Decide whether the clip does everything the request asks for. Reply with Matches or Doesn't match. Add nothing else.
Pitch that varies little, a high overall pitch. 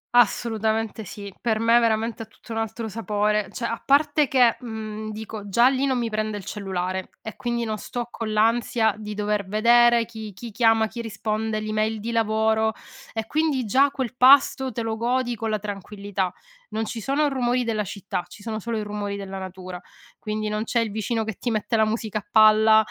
Matches